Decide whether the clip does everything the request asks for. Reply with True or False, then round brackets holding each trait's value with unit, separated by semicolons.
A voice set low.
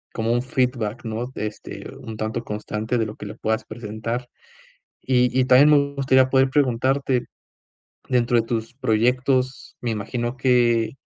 True (120 Hz)